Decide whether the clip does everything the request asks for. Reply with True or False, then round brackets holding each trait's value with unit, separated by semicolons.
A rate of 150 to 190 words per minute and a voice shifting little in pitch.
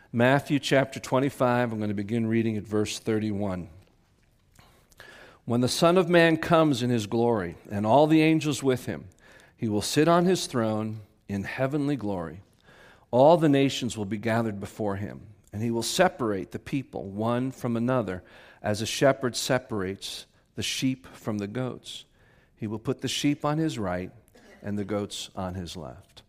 False (170 wpm; 4.4 semitones)